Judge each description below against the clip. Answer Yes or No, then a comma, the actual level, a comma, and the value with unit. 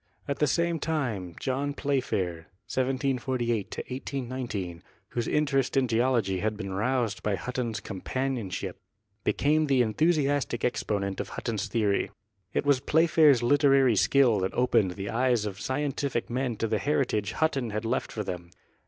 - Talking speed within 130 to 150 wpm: Yes, average, 145 wpm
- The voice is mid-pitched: No, low, 125 Hz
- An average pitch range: Yes, average, 4.5 semitones